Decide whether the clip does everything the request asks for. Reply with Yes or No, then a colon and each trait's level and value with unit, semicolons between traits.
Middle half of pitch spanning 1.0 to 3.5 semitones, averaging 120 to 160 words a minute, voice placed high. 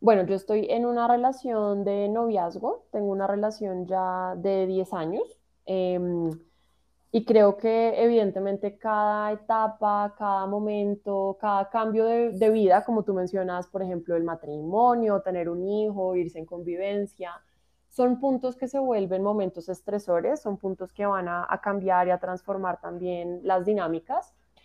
Yes: average, 2.8 semitones; average, 150 wpm; high, 200 Hz